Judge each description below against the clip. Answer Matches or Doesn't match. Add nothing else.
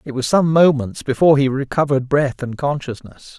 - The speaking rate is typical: Matches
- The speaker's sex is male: Matches